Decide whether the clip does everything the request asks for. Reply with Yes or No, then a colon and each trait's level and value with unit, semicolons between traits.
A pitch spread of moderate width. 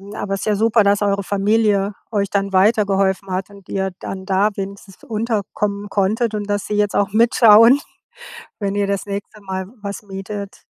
No: narrow, 1.2 semitones